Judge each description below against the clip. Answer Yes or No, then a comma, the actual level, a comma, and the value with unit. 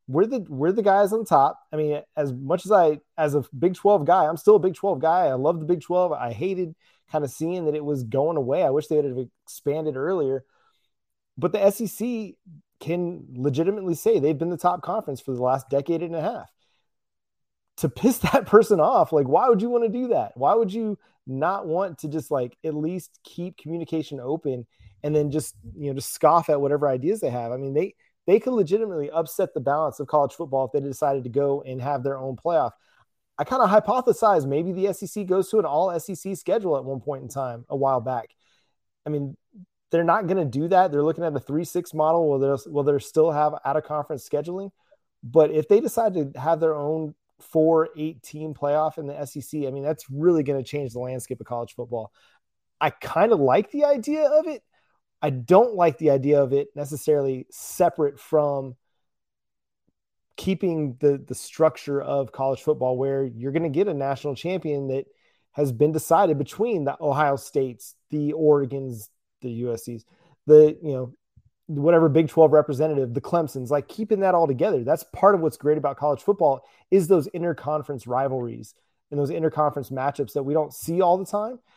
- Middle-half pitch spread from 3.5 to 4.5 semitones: Yes, average, 4.2 semitones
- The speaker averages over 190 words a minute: Yes, average, 200 wpm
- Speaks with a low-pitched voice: No, medium, 155 Hz